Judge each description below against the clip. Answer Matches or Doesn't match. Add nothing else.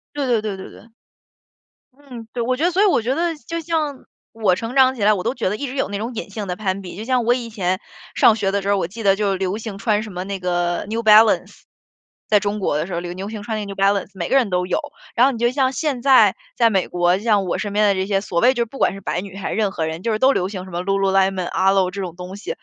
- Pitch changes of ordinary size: Matches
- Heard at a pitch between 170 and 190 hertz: Doesn't match